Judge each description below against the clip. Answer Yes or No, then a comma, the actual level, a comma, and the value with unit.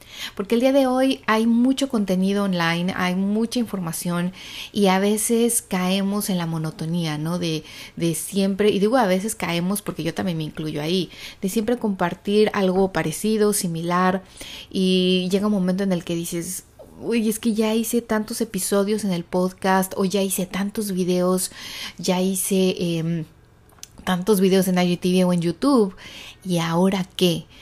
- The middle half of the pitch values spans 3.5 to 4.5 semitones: No, average, 2.9 semitones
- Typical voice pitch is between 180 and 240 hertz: Yes, high, 190 Hz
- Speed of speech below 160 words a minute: No, average, 165 wpm